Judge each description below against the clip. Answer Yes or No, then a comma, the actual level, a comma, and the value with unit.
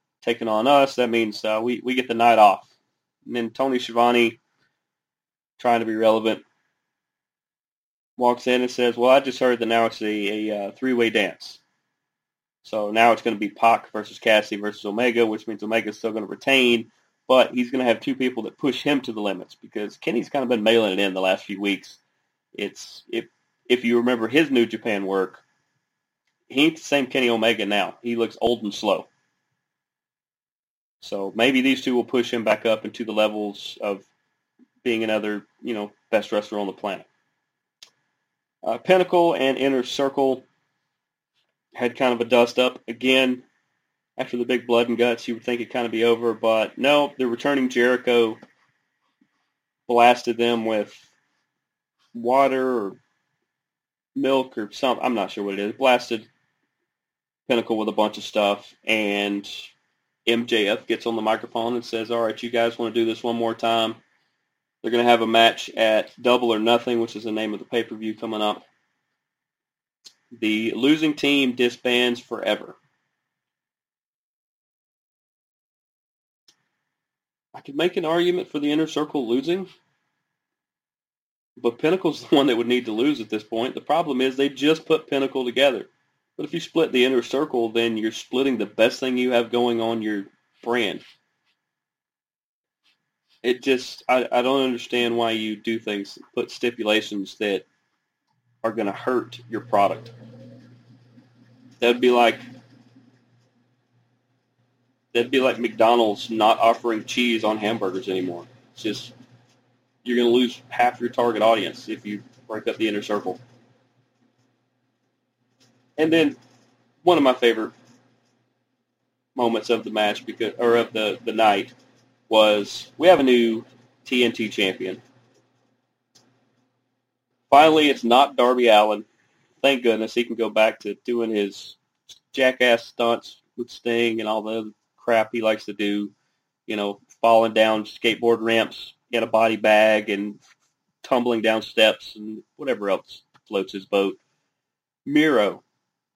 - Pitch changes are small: Yes, narrow, 2.3 semitones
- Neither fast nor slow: Yes, average, 160 wpm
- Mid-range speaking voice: No, low, 120 Hz